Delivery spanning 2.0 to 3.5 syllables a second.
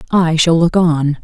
No: 4.0 syllables/s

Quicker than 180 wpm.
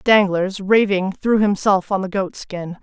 No: average, 170 wpm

